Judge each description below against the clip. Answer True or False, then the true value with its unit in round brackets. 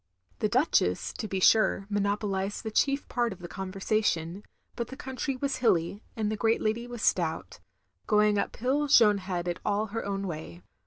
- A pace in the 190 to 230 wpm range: False (180 wpm)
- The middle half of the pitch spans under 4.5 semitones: True (3.4 semitones)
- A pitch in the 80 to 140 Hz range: False (210 Hz)